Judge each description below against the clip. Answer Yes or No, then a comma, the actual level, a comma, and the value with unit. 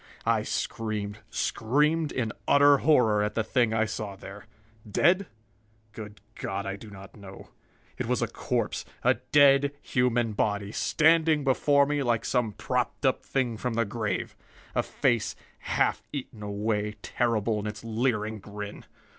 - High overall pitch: No, low, 115 Hz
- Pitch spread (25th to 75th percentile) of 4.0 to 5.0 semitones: Yes, average, 4.3 semitones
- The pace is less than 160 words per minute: Yes, average, 150 wpm